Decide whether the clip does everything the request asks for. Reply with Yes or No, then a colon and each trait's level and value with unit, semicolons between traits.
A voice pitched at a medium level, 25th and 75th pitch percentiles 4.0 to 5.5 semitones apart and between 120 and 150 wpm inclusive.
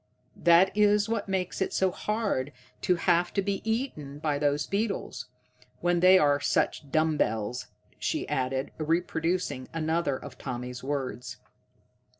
Yes: medium, 165 Hz; average, 5.2 semitones; average, 140 wpm